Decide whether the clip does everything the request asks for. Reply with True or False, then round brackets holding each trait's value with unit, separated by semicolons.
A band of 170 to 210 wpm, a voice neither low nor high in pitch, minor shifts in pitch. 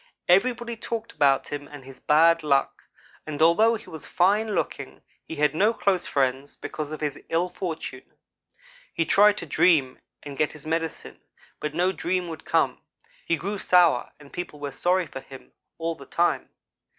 False (175 wpm; 165 Hz; 4.0 semitones)